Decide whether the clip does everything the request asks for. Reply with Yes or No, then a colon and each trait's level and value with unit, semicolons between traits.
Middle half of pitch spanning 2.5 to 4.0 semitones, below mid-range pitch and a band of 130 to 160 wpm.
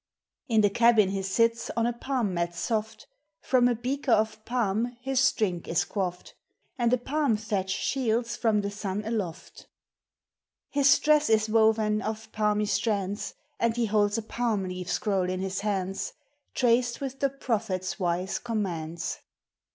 No: average, 3.5 semitones; high, 220 Hz; average, 155 wpm